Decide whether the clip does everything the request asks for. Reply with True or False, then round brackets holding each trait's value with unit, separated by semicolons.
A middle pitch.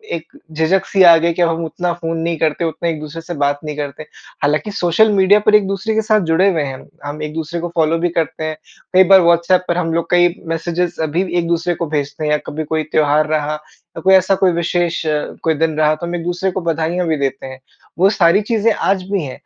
True (170 Hz)